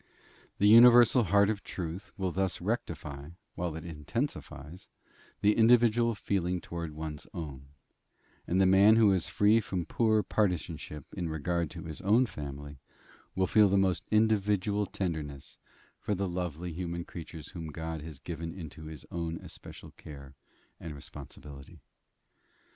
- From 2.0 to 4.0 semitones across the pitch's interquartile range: No, average, 4.5 semitones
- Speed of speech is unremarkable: Yes, average, 145 wpm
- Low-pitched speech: Yes, very low, 90 Hz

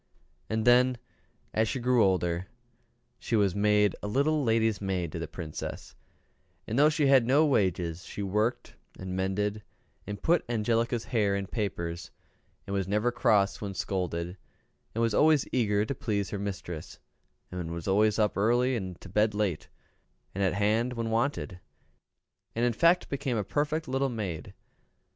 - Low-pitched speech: Yes, low, 105 Hz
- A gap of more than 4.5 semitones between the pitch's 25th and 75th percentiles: No, average, 4.1 semitones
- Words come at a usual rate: Yes, average, 160 wpm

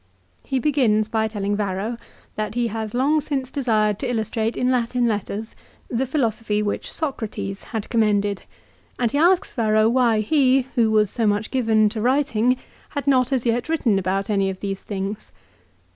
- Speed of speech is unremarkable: Yes, average, 170 wpm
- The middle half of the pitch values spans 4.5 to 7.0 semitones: No, average, 3.3 semitones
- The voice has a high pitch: Yes, high, 225 Hz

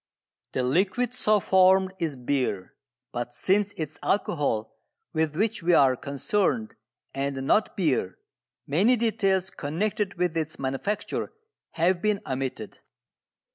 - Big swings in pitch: Yes, wide, 6.7 semitones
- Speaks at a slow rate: Yes, slow, 125 wpm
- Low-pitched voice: No, medium, 170 Hz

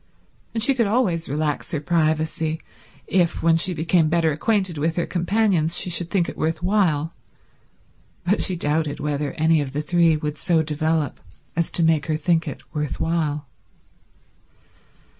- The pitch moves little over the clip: Yes, narrow, 2.3 semitones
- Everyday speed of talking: Yes, average, 160 wpm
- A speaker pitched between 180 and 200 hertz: No, medium, 160 Hz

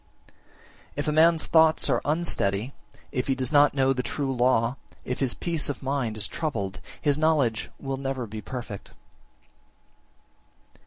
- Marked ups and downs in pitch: No, average, 3.6 semitones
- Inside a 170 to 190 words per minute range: No, average, 155 wpm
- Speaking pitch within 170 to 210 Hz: No, low, 135 Hz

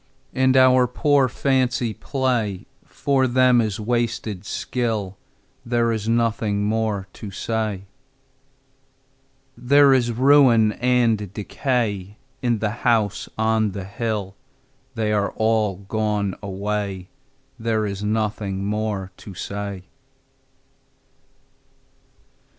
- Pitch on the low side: Yes, low, 110 Hz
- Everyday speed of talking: No, slow, 100 wpm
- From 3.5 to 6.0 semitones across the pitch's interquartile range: No, average, 3.0 semitones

